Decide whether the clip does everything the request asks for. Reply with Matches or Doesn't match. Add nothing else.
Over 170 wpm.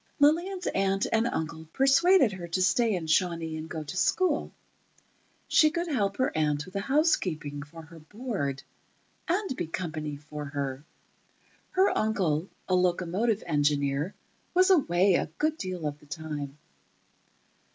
Doesn't match